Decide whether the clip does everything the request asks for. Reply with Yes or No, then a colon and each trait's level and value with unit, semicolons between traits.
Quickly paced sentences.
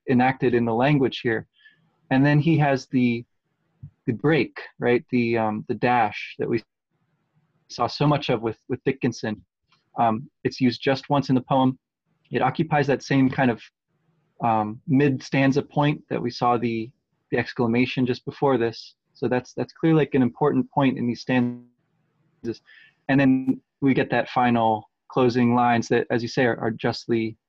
No: average, 170 wpm